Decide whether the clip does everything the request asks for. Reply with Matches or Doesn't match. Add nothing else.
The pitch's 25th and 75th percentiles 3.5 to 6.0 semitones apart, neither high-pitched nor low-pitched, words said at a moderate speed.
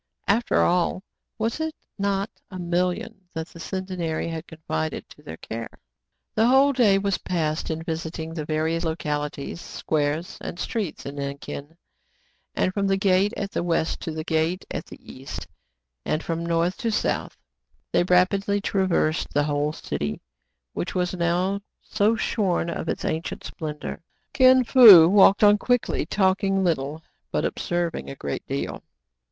Matches